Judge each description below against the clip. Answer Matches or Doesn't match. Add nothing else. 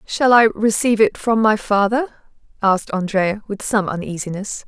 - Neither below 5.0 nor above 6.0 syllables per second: Matches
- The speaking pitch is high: Matches